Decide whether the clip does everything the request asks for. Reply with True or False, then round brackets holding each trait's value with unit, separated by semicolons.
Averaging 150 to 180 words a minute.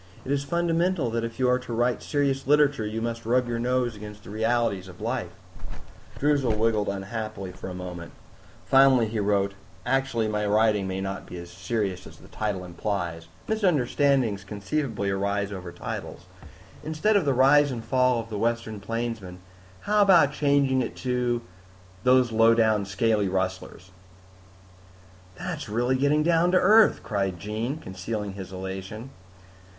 True (155 wpm)